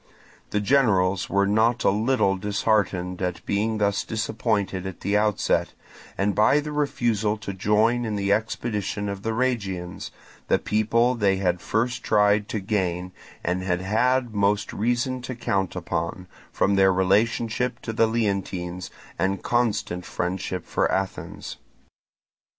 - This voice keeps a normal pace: Yes, average, 145 wpm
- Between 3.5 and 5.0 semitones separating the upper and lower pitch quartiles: No, average, 2.9 semitones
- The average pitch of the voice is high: No, low, 105 Hz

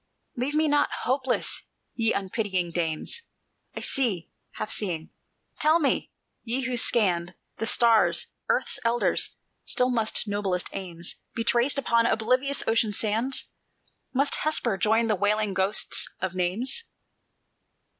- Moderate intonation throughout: Yes, average, 4.9 semitones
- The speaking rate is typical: No, slow, 125 wpm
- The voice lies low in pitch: No, high, 225 Hz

